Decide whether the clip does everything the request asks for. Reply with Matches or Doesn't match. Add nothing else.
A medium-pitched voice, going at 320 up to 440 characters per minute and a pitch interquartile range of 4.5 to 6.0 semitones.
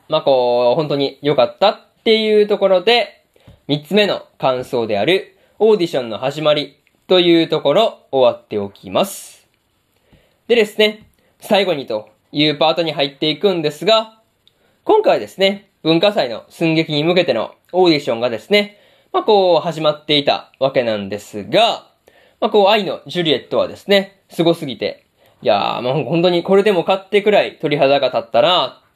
Matches